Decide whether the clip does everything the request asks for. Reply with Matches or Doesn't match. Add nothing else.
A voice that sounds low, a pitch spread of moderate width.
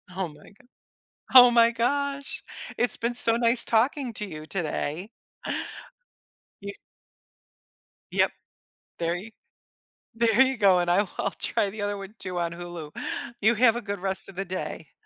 Doesn't match